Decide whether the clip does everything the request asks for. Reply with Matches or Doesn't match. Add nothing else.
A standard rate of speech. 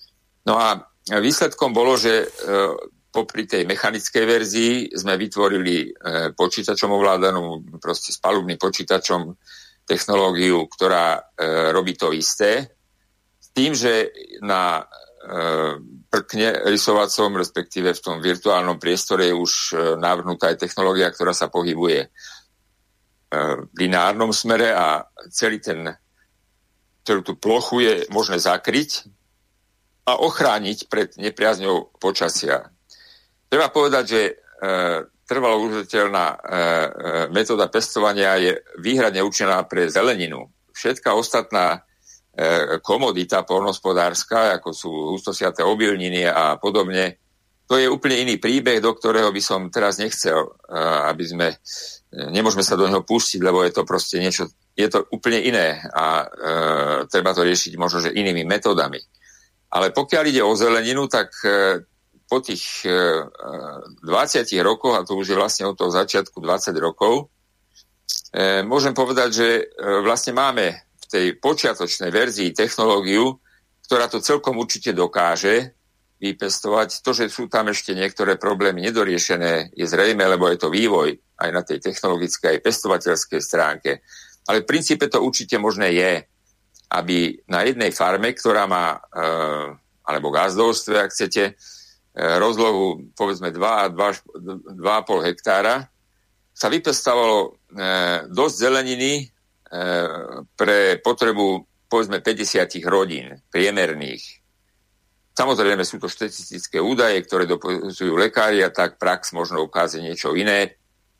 Matches